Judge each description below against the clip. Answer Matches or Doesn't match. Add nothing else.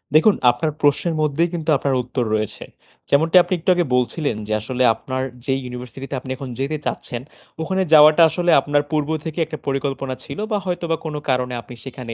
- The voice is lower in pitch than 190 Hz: Matches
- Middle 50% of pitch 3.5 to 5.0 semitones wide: Matches